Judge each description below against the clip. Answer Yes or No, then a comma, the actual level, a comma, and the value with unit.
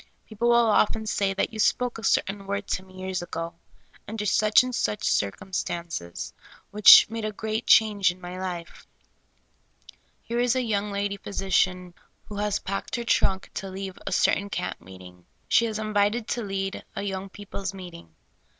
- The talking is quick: No, average, 175 wpm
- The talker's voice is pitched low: No, high, 200 Hz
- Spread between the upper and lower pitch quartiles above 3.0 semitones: No, narrow, 2.6 semitones